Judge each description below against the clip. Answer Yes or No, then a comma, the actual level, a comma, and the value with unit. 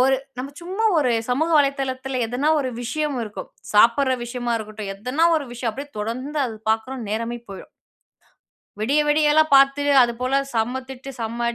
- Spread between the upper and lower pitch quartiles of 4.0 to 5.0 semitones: No, average, 3.4 semitones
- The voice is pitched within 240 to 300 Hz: Yes, very high, 255 Hz